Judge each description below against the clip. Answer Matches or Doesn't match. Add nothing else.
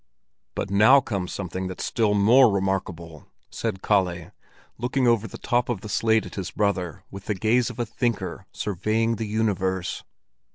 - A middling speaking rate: Matches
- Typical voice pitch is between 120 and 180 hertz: Doesn't match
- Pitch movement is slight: Doesn't match